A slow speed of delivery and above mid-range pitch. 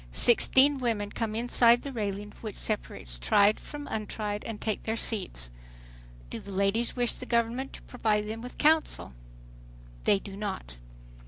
No: average, 155 wpm; high, 220 Hz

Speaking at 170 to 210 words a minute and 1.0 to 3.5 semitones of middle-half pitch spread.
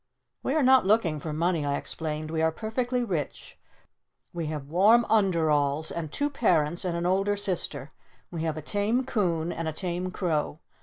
No: average, 175 wpm; average, 4.6 semitones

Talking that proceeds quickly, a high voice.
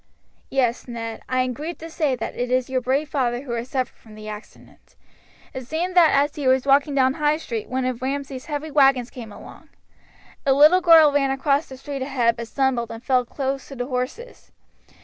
Yes: fast, 210 wpm; very high, 265 Hz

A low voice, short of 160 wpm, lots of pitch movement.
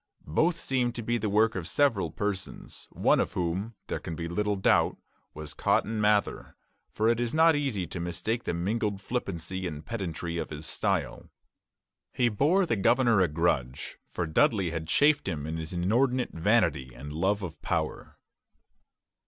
No: low, 100 Hz; average, 170 wpm; wide, 5.9 semitones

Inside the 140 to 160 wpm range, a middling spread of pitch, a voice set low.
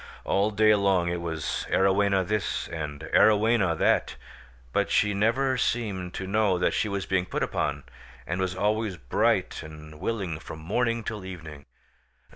Yes: average, 155 wpm; average, 3.8 semitones; very low, 95 Hz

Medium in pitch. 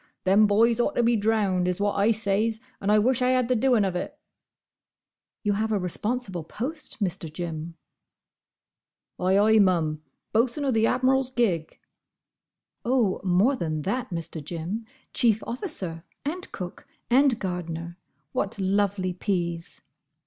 No: high, 205 Hz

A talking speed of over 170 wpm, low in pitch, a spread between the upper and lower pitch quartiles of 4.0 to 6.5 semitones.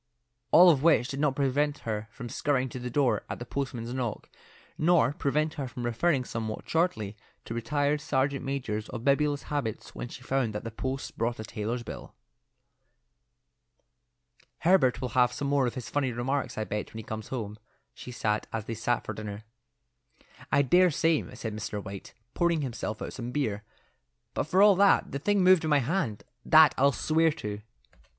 Yes: average, 185 wpm; low, 130 Hz; average, 4.4 semitones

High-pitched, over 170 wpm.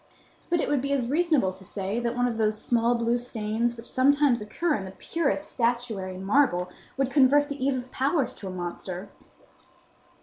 Yes: high, 240 Hz; average, 190 wpm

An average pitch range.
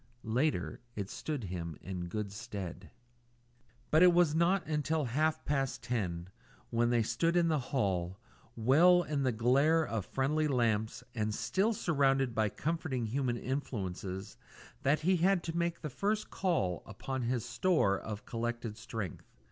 No: wide, 6.9 semitones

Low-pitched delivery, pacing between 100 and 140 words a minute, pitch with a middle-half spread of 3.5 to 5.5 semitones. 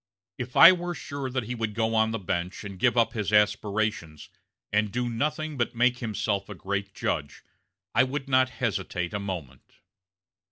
No: low, 110 Hz; average, 175 wpm; average, 4.1 semitones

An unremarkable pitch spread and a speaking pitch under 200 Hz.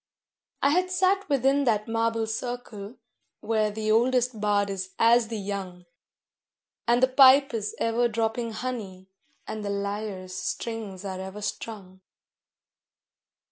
No: average, 3.3 semitones; high, 220 Hz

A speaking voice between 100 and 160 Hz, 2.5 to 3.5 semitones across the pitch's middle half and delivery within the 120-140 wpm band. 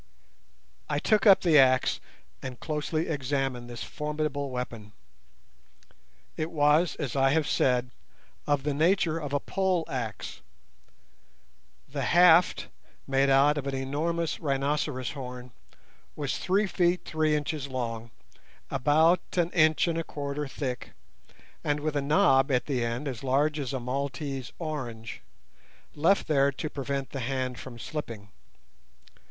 Yes: medium, 140 Hz; average, 3.2 semitones; slow, 135 wpm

